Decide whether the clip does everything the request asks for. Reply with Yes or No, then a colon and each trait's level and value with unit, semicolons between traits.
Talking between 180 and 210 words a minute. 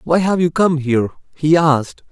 Yes: average, 200 wpm